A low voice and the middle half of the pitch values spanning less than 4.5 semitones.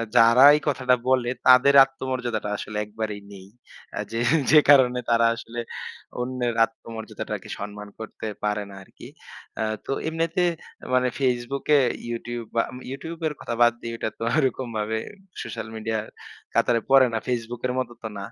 Yes: low, 120 Hz; narrow, 2.6 semitones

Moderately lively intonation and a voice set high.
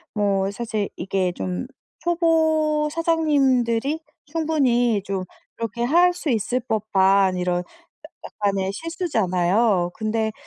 No: wide, 7.7 semitones; high, 230 Hz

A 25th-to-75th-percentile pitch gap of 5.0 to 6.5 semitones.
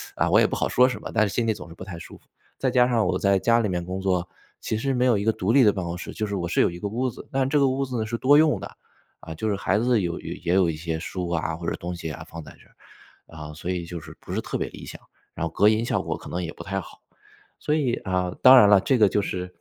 Yes: wide, 5.4 semitones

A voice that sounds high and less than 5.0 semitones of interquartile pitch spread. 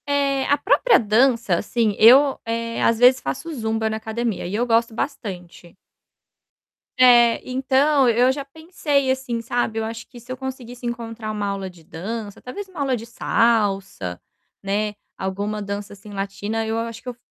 Yes: high, 230 Hz; average, 3.6 semitones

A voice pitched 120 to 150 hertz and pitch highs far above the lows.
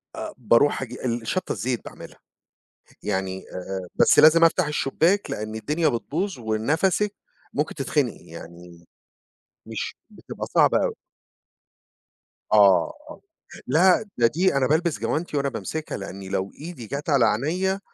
Yes: medium, 140 Hz; wide, 7.3 semitones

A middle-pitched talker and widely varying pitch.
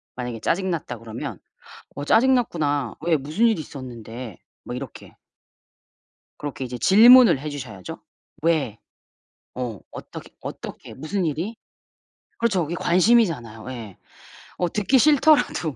Yes: medium, 150 Hz; wide, 8.1 semitones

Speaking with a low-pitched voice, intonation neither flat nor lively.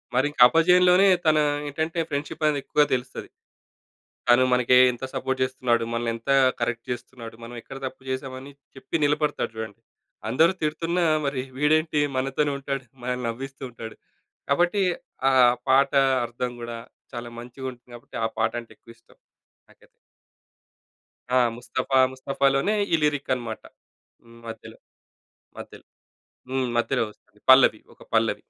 Yes: low, 130 Hz; average, 3.4 semitones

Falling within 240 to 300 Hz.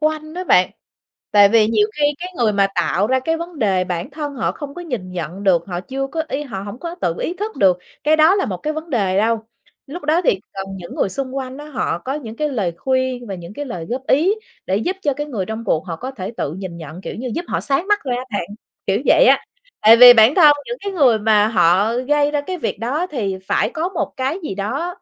Yes: very high, 250 Hz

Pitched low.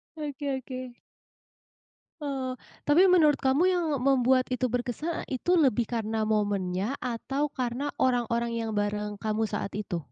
No: very high, 250 Hz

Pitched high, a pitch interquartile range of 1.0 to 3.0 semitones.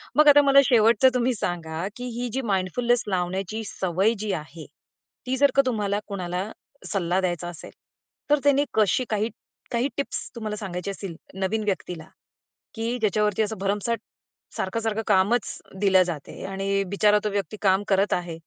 No: high, 205 Hz; average, 3.6 semitones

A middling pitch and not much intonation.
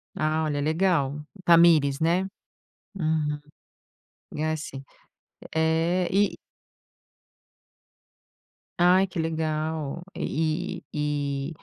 Yes: medium, 160 Hz; narrow, 2.3 semitones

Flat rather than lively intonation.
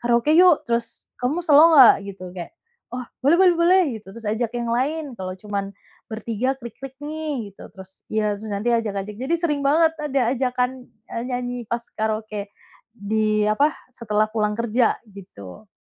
No: average, 4.4 semitones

